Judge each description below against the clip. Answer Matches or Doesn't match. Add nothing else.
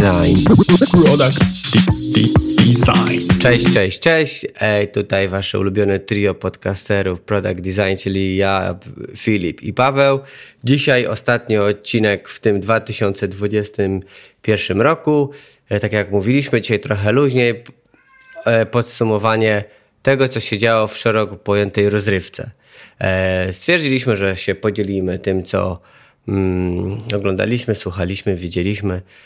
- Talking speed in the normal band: Doesn't match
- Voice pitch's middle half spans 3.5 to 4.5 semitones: Doesn't match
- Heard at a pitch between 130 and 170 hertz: Doesn't match